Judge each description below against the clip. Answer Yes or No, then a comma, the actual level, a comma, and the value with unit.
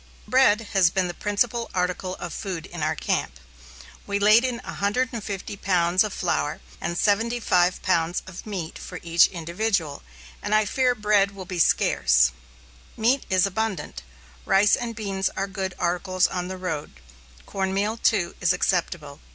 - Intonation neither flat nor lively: Yes, average, 3.3 semitones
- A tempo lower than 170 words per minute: Yes, average, 150 wpm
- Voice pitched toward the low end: No, high, 190 Hz